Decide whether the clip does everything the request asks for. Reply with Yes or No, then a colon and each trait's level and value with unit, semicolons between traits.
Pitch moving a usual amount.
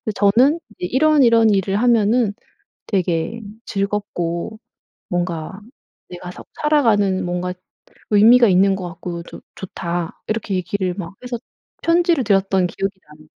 Yes: average, 4.3 semitones